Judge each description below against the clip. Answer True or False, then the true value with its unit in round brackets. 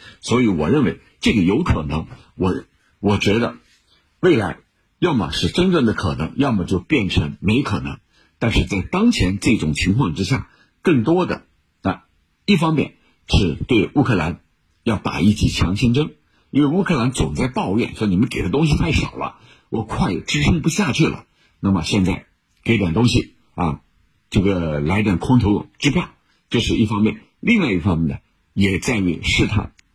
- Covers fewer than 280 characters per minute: True (245 characters per minute)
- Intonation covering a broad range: False (4.9 semitones)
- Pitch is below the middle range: True (100 Hz)